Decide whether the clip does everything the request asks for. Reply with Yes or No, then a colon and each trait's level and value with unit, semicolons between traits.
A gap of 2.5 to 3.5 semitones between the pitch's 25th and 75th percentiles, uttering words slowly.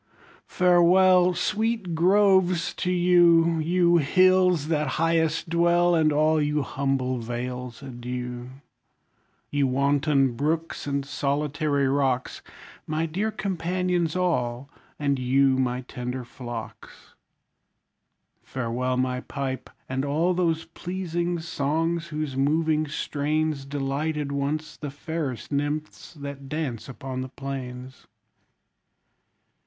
No: average, 4.0 semitones; slow, 105 wpm